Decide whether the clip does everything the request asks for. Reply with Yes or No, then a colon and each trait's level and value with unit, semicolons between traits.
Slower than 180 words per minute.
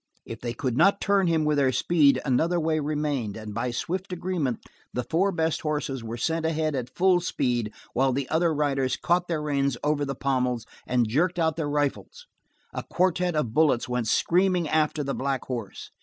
No: average, 190 wpm